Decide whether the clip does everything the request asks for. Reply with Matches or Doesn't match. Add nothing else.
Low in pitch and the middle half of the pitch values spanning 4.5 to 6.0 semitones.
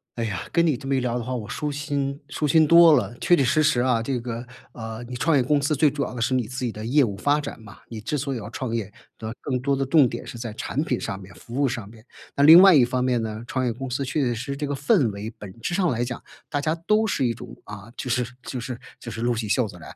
Doesn't match